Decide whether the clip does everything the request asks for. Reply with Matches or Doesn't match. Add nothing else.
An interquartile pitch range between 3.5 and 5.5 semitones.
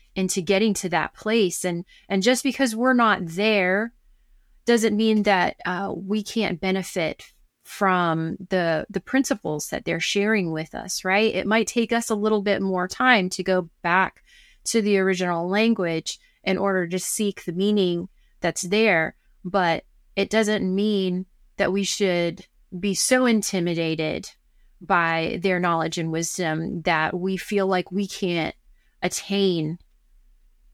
Doesn't match